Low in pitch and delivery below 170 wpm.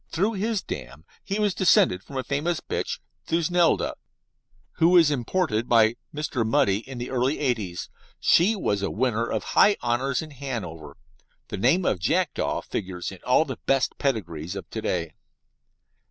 Yes: low, 130 Hz; average, 160 wpm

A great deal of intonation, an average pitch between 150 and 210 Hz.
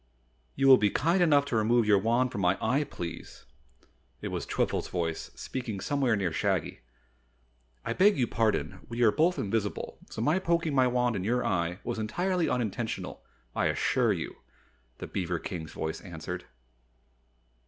No: wide, 6.1 semitones; low, 115 Hz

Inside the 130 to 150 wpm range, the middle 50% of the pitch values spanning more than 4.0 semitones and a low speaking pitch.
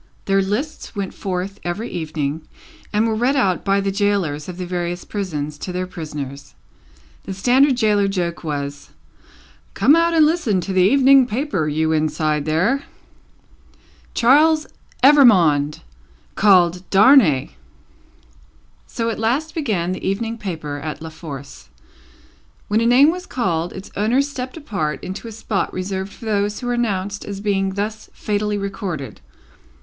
No: average, 145 wpm; average, 5.3 semitones; high, 195 Hz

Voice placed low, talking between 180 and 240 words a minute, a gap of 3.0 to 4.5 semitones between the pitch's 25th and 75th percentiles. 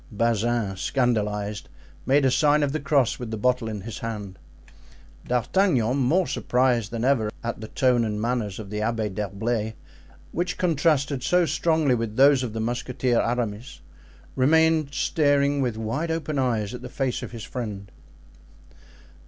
No: low, 125 Hz; average, 155 wpm; average, 4.2 semitones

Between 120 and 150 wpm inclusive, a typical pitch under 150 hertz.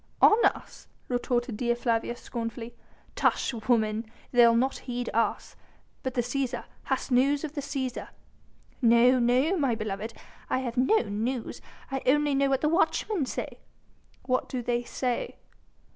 No: average, 145 wpm; high, 245 Hz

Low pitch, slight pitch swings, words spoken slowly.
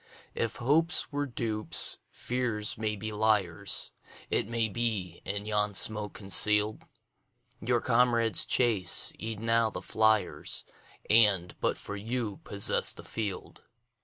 Yes: low, 110 Hz; narrow, 2.1 semitones; slow, 110 wpm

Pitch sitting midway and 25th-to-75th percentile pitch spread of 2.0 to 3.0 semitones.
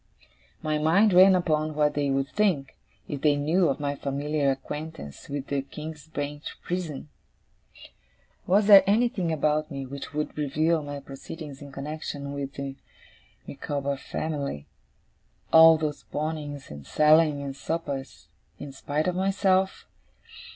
Yes: medium, 150 Hz; narrow, 2.4 semitones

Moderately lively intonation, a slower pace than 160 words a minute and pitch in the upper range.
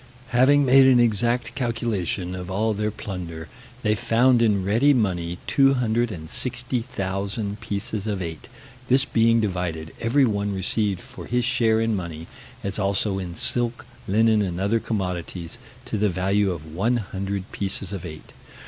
No: average, 3.9 semitones; average, 145 wpm; low, 105 Hz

